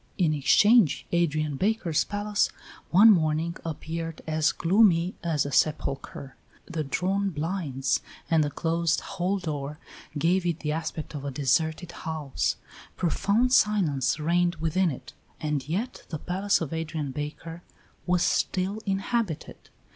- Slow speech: Yes, slow, 130 wpm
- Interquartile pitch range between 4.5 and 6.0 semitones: No, average, 3.6 semitones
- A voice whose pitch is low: No, medium, 165 Hz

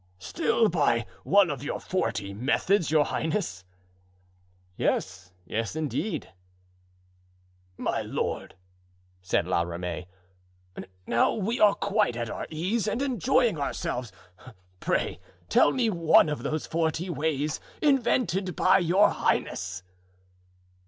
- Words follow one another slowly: Yes, slow, 110 wpm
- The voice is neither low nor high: Yes, medium, 160 Hz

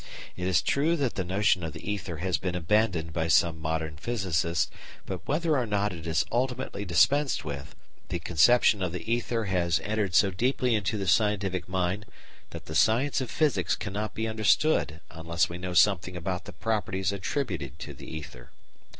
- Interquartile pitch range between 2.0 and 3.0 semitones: No, average, 4.7 semitones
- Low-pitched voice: Yes, very low, 95 Hz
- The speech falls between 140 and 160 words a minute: No, average, 180 wpm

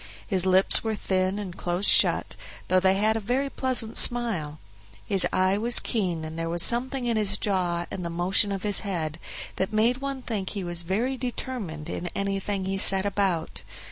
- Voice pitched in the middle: No, high, 195 Hz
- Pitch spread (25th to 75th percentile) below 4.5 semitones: Yes, average, 3.8 semitones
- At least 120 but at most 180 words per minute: No, average, 190 wpm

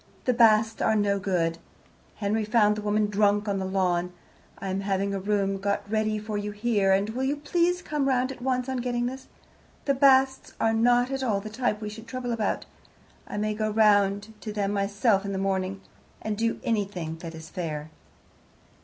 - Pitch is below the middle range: No, high, 210 Hz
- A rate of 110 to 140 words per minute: No, average, 195 wpm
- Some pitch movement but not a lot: Yes, average, 3.3 semitones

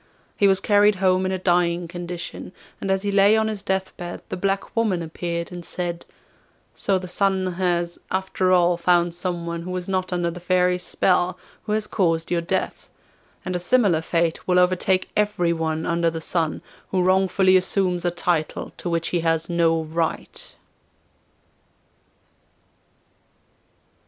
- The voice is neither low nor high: Yes, medium, 180 Hz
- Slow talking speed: No, average, 155 wpm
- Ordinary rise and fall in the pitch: No, narrow, 1.8 semitones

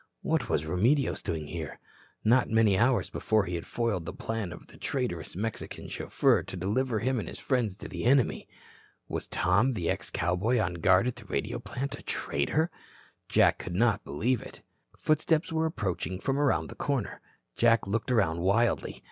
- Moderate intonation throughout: No, wide, 5.8 semitones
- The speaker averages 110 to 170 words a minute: No, average, 180 wpm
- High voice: No, low, 110 Hz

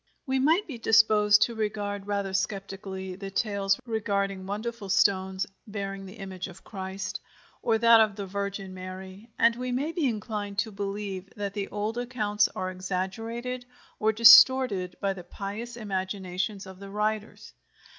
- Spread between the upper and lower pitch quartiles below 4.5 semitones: Yes, narrow, 2.5 semitones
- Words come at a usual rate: Yes, average, 155 wpm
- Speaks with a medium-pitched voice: No, high, 205 Hz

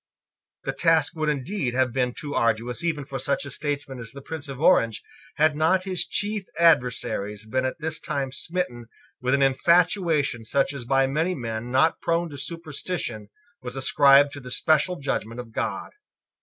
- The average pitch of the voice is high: No, medium, 140 Hz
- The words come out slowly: No, average, 175 wpm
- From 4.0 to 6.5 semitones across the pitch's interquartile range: Yes, average, 4.4 semitones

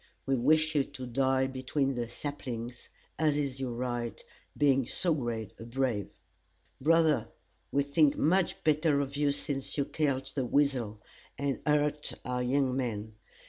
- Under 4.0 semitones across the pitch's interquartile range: Yes, average, 2.8 semitones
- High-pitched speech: No, low, 135 Hz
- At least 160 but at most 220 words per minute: No, average, 150 wpm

